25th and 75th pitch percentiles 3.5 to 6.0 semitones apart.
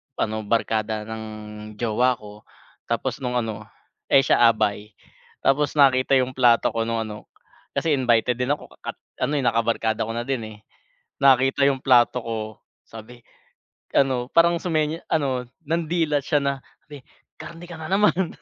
Yes: average, 4.2 semitones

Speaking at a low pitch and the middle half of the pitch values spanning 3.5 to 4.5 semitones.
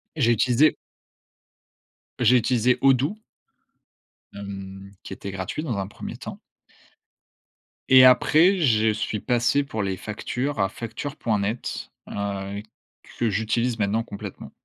Yes: low, 115 Hz; average, 4.0 semitones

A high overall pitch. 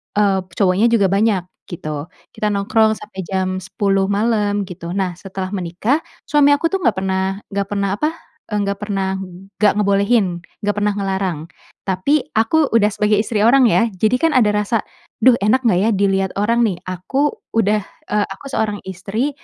Yes: high, 205 Hz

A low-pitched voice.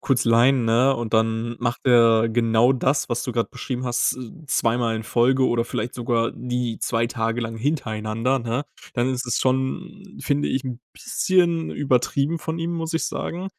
Yes: low, 125 Hz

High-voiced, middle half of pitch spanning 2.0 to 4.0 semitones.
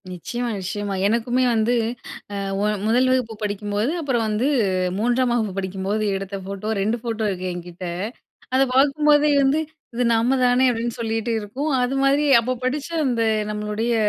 Yes: high, 230 Hz; average, 3.6 semitones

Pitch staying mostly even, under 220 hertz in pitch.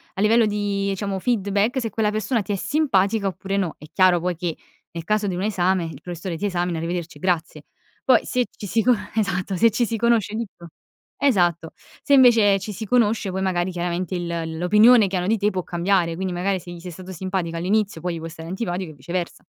No: average, 3.3 semitones; high, 190 Hz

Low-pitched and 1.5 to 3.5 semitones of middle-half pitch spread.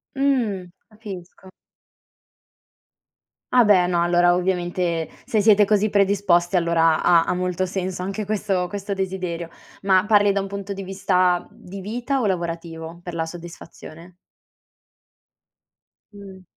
No: medium, 185 Hz; narrow, 2.5 semitones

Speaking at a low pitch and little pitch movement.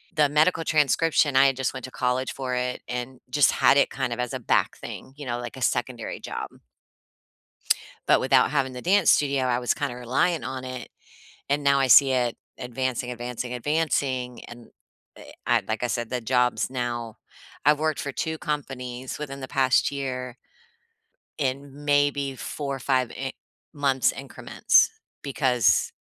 Yes: low, 130 Hz; narrow, 2.3 semitones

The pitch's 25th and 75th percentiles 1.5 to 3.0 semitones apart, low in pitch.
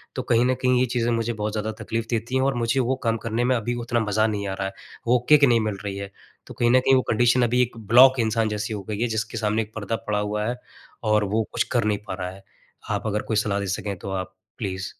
Yes: narrow, 2.6 semitones; low, 110 Hz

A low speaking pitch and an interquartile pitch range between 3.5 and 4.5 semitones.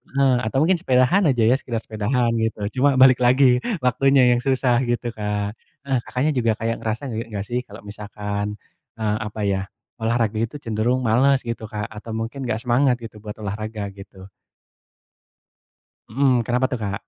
No: low, 115 Hz; average, 3.1 semitones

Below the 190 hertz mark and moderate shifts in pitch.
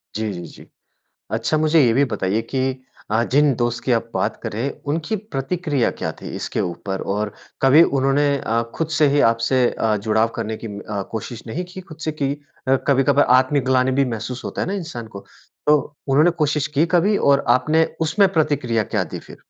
Yes: low, 135 Hz; average, 5.0 semitones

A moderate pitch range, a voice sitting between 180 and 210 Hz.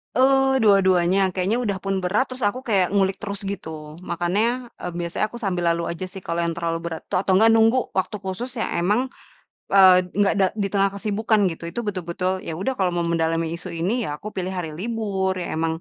Yes: average, 3.5 semitones; high, 190 Hz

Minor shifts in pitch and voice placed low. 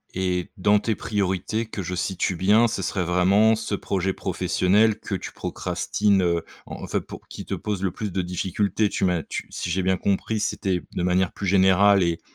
Yes: narrow, 2.2 semitones; very low, 95 Hz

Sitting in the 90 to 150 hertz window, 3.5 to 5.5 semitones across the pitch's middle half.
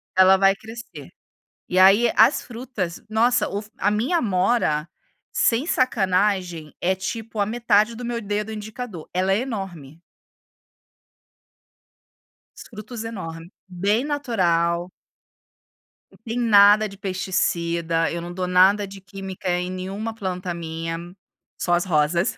No: high, 195 Hz; average, 3.8 semitones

